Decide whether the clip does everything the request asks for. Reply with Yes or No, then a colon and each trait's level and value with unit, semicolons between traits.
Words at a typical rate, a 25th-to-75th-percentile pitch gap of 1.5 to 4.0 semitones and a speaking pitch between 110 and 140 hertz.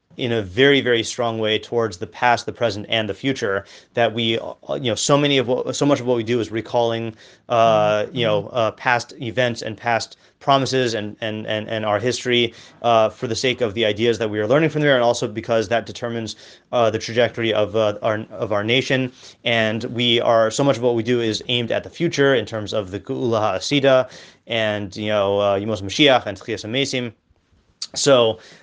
No: fast, 210 wpm; narrow, 2.4 semitones; low, 115 Hz